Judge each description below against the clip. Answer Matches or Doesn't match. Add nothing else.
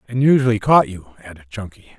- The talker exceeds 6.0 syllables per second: Matches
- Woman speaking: Doesn't match